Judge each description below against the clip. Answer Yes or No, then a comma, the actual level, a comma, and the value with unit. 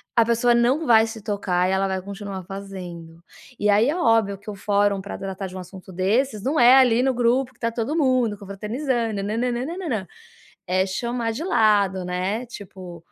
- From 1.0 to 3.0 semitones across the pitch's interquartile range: No, average, 3.9 semitones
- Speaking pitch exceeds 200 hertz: Yes, high, 210 Hz